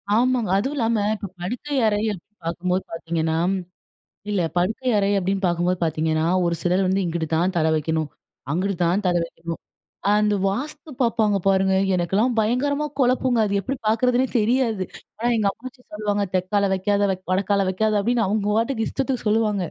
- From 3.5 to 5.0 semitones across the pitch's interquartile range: Yes, average, 4.2 semitones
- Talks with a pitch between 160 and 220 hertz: Yes, high, 205 Hz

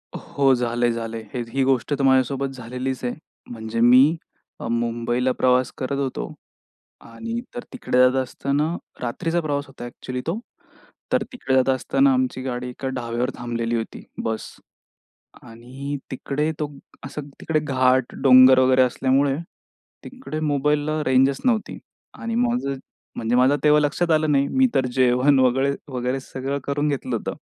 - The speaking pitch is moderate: No, low, 130 Hz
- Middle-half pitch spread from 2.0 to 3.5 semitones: Yes, average, 2.7 semitones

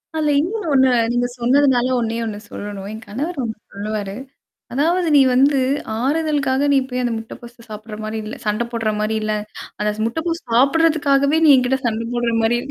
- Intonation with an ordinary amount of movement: Yes, average, 4.6 semitones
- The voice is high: Yes, high, 245 Hz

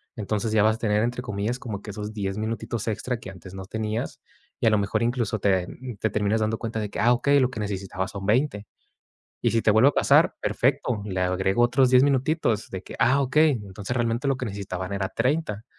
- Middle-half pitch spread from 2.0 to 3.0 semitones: No, average, 3.5 semitones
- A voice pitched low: Yes, low, 110 Hz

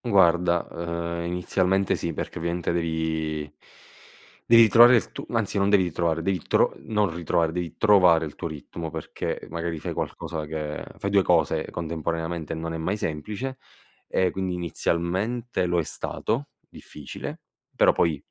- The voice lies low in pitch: Yes, very low, 85 Hz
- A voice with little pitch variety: No, average, 3.2 semitones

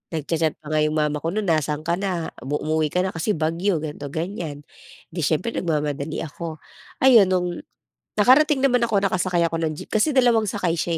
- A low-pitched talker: No, medium, 170 Hz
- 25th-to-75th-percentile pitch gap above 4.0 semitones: Yes, average, 4.5 semitones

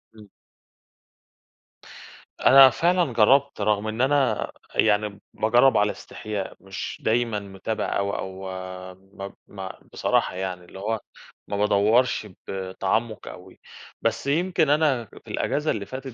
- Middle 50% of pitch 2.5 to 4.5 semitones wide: No, average, 5.0 semitones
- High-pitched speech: No, low, 110 Hz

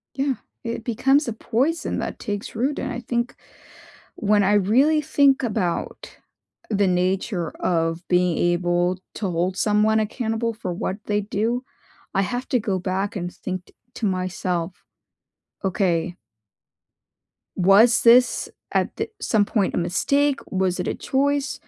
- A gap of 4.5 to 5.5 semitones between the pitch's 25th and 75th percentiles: Yes, average, 4.9 semitones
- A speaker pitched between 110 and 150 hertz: No, high, 205 Hz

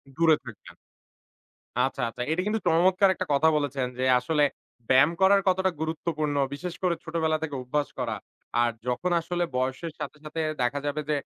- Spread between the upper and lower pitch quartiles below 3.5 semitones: No, average, 3.9 semitones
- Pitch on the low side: No, medium, 155 Hz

